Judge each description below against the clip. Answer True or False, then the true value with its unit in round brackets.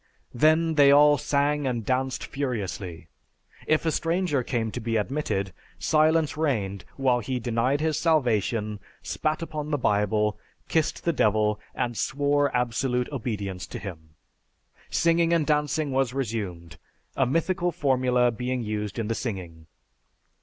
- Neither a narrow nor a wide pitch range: False (5.7 semitones)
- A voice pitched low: True (125 Hz)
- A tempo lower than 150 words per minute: True (140 wpm)